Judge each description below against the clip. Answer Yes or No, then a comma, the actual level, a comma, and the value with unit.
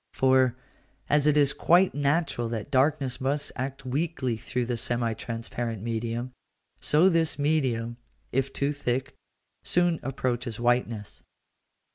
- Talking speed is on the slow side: Yes, slow, 125 wpm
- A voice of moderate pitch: No, low, 130 Hz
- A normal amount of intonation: Yes, average, 3.5 semitones